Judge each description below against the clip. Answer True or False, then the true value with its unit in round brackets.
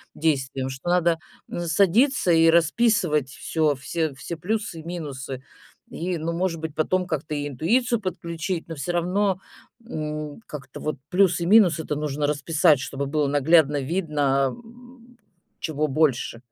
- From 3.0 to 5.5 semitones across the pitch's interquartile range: True (3.7 semitones)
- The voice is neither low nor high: True (160 Hz)